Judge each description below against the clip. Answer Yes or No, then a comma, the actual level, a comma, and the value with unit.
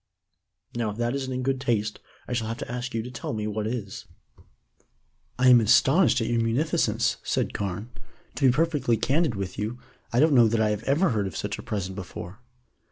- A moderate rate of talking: No, fast, 210 wpm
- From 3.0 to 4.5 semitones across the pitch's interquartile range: Yes, average, 3.3 semitones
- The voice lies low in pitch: Yes, low, 115 Hz